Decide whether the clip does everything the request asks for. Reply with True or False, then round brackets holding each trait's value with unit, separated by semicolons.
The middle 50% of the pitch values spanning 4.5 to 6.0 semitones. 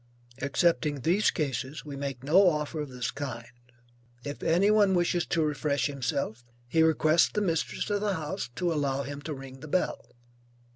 False (3.9 semitones)